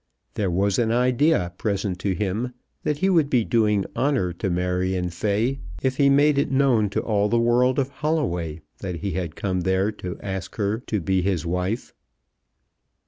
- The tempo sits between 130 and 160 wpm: No, average, 180 wpm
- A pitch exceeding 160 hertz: No, low, 105 Hz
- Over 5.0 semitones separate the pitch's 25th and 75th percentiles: Yes, wide, 5.5 semitones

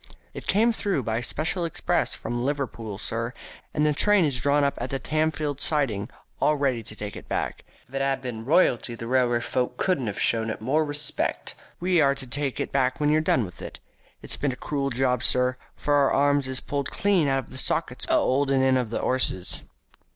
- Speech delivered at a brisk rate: Yes, fast, 215 wpm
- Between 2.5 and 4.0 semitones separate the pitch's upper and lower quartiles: Yes, average, 3.2 semitones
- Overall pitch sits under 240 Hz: Yes, low, 135 Hz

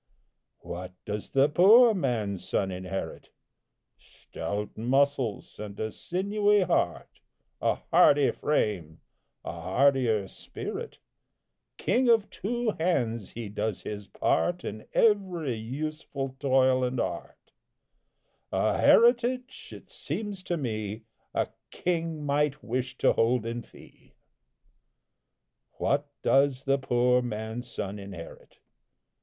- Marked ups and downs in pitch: Yes, wide, 7.5 semitones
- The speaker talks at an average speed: No, slow, 110 wpm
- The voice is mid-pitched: No, low, 130 Hz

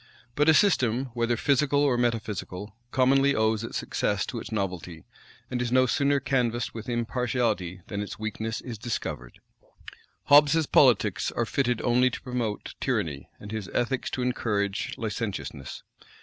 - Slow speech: No, average, 150 wpm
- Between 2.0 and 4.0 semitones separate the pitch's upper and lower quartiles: Yes, average, 3.3 semitones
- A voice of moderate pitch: No, low, 120 Hz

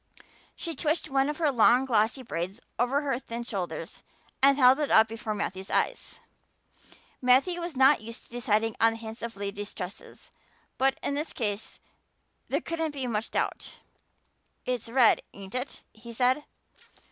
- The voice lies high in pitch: Yes, high, 245 Hz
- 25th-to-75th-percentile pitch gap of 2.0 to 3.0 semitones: No, average, 3.7 semitones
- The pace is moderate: Yes, average, 160 wpm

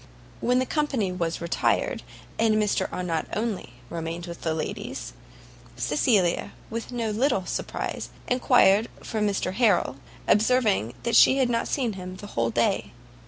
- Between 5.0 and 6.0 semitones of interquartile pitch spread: Yes, wide, 5.4 semitones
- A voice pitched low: No, high, 210 Hz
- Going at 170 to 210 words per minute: No, average, 145 wpm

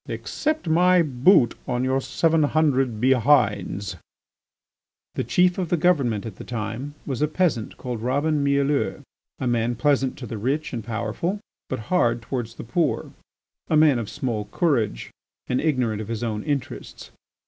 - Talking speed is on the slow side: No, average, 160 wpm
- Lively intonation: No, average, 4.9 semitones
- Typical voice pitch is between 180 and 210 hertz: No, low, 130 Hz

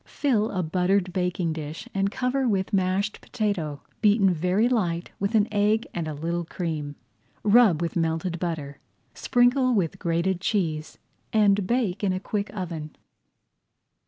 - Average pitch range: Yes, average, 4.0 semitones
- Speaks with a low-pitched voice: No, medium, 185 Hz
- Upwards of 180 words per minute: No, average, 155 wpm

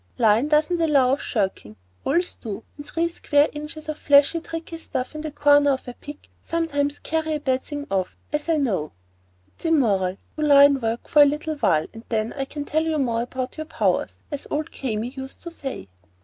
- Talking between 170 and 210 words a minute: Yes, average, 195 wpm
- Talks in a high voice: Yes, very high, 285 Hz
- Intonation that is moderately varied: Yes, average, 3.9 semitones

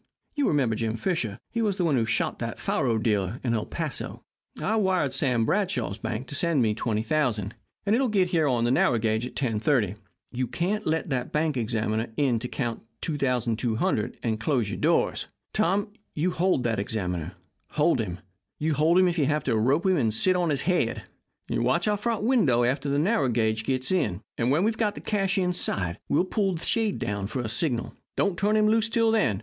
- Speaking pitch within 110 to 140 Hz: Yes, low, 135 Hz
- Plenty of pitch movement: Yes, wide, 8.2 semitones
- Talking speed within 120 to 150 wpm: No, fast, 205 wpm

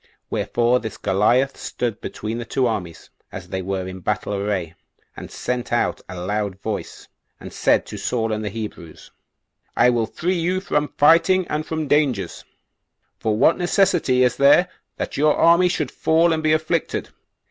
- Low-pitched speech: Yes, low, 120 Hz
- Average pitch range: No, wide, 7.1 semitones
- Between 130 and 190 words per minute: Yes, average, 165 wpm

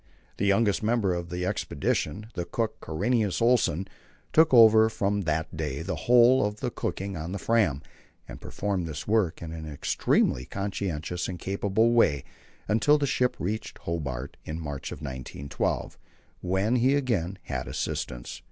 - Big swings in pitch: Yes, wide, 5.8 semitones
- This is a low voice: Yes, very low, 95 Hz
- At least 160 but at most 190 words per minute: No, average, 150 wpm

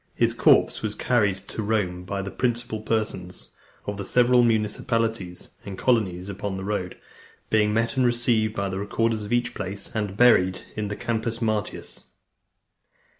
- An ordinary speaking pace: Yes, average, 160 wpm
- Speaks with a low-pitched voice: Yes, low, 110 Hz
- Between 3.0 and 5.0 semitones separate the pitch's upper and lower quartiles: No, narrow, 2.5 semitones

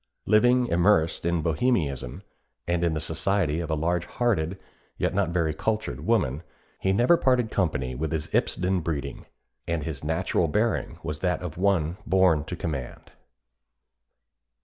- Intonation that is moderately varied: Yes, average, 3.9 semitones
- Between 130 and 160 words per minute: Yes, average, 150 wpm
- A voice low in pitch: Yes, very low, 85 Hz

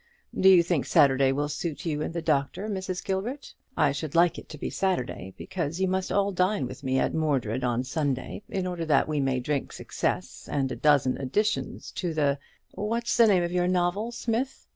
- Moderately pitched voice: Yes, medium, 165 Hz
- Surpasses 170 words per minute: Yes, fast, 205 wpm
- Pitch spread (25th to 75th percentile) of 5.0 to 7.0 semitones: Yes, average, 5.3 semitones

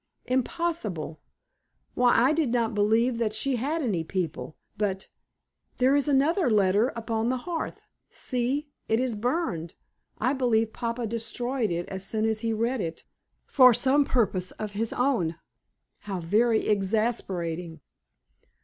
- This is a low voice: No, high, 230 Hz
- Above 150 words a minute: No, average, 140 wpm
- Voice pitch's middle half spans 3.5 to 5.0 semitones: Yes, average, 4.1 semitones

